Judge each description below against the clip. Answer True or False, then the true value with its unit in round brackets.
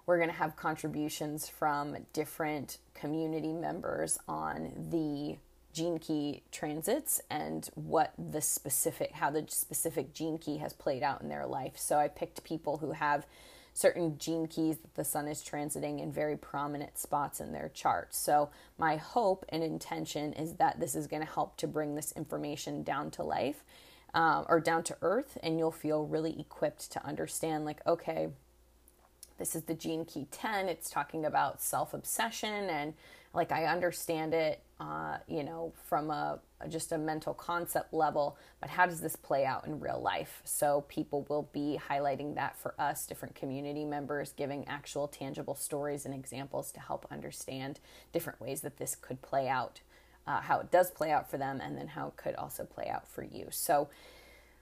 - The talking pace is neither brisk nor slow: True (180 wpm)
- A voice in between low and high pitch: True (150 Hz)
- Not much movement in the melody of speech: True (2.0 semitones)